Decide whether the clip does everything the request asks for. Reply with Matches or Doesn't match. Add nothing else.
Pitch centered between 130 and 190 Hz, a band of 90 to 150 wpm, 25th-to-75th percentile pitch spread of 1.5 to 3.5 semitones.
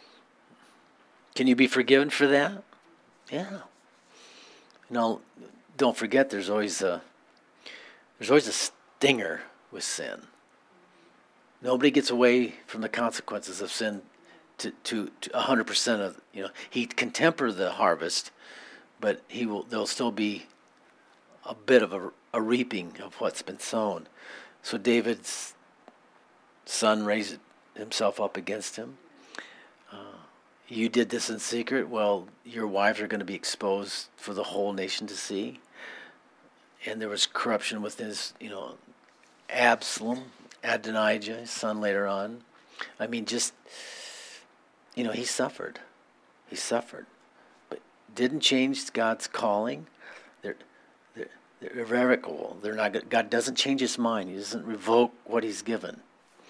Doesn't match